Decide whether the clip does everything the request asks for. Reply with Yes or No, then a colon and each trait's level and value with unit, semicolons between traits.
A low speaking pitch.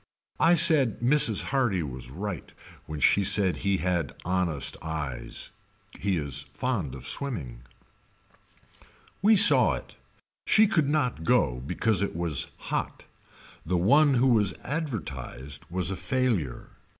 Yes: very low, 95 Hz